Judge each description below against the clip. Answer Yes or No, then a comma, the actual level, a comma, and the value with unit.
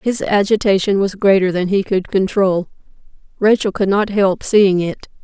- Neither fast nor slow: Yes, average, 160 wpm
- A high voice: Yes, high, 195 Hz